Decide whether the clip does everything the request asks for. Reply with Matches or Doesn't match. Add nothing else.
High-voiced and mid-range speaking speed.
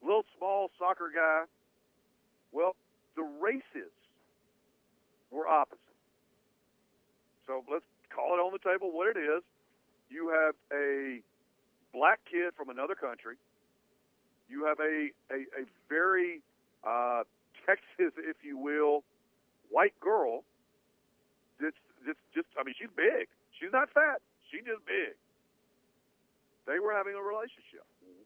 Doesn't match